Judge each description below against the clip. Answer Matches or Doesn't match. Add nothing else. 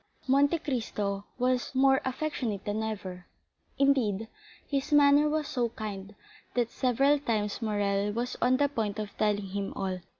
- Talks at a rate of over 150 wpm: Doesn't match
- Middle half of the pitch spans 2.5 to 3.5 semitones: Doesn't match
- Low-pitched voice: Doesn't match